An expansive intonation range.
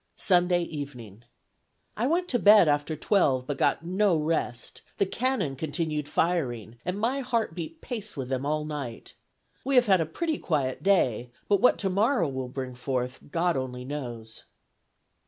Yes: wide, 7.3 semitones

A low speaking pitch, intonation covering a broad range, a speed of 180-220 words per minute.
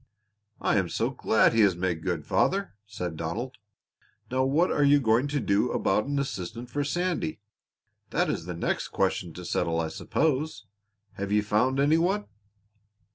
No: low, 115 Hz; wide, 7.3 semitones; average, 170 wpm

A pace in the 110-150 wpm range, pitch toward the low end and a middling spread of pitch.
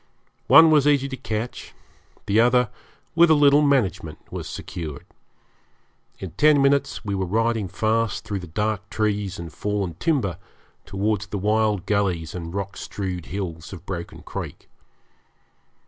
Yes: average, 145 wpm; low, 105 Hz; average, 4.7 semitones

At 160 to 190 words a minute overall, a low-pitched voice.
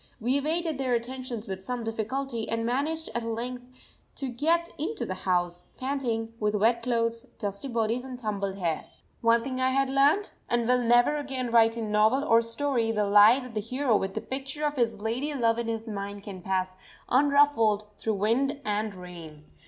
No: average, 185 wpm; high, 235 Hz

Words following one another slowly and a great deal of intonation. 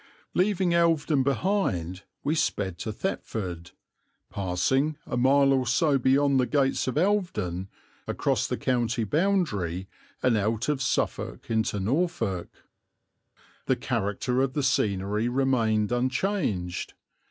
Yes: slow, 120 wpm; wide, 6.3 semitones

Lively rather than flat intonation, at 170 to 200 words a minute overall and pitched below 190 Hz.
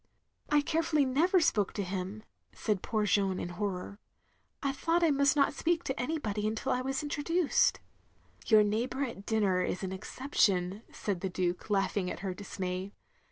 No: wide, 6.7 semitones; average, 175 wpm; high, 215 Hz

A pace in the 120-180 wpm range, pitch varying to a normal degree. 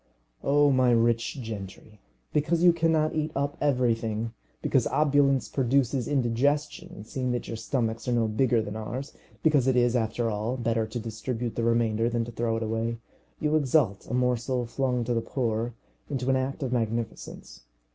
Yes: average, 170 wpm; average, 3.3 semitones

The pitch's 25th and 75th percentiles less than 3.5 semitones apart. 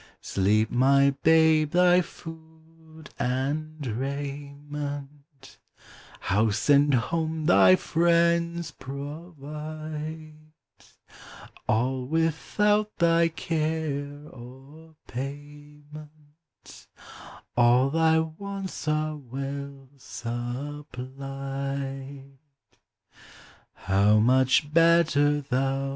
Yes: average, 2.9 semitones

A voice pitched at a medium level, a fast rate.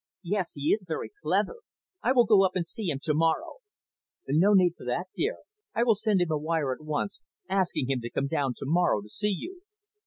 Yes: medium, 175 Hz; fast, 220 wpm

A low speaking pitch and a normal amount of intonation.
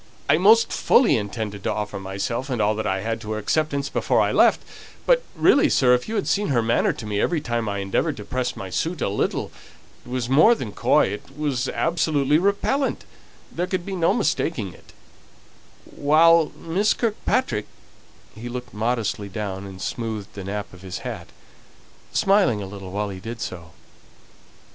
No: low, 120 Hz; wide, 8.1 semitones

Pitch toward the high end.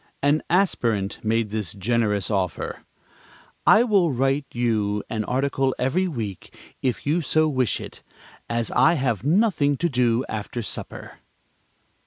No: low, 125 Hz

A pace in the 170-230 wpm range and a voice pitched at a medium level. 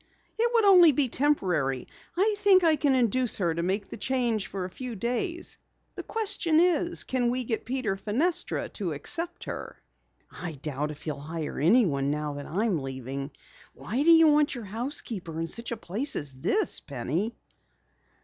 No: average, 180 wpm; high, 230 Hz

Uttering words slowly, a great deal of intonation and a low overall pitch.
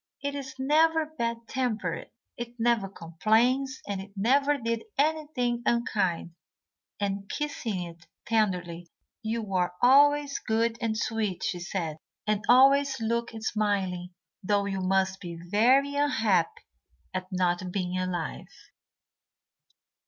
No: slow, 120 wpm; wide, 5.7 semitones; high, 220 Hz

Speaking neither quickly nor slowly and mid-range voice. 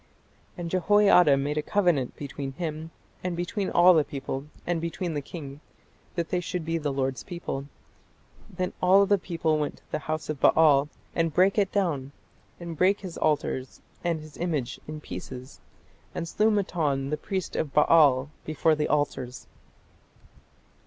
Yes: average, 160 wpm; medium, 160 Hz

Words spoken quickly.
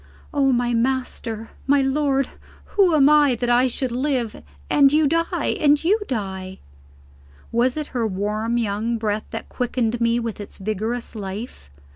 No: average, 155 wpm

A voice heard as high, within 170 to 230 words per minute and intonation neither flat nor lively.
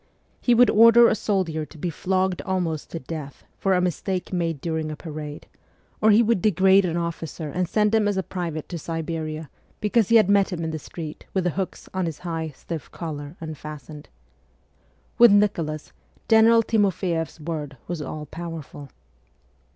No: medium, 170 Hz; average, 175 wpm; average, 3.8 semitones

